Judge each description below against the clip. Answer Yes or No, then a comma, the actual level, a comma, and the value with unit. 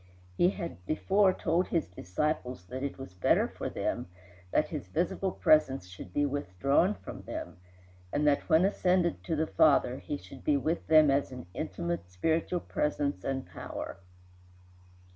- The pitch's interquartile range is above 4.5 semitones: Yes, average, 5.0 semitones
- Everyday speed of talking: Yes, average, 160 wpm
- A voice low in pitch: No, medium, 145 Hz